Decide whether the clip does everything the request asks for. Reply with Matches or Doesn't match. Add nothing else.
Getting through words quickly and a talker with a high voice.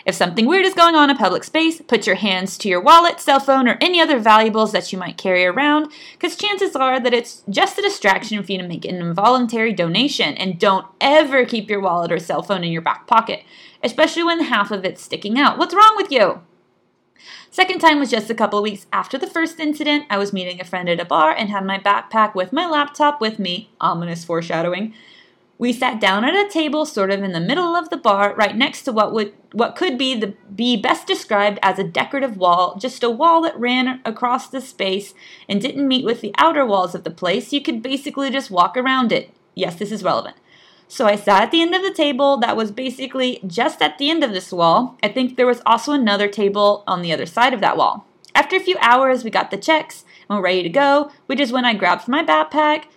Matches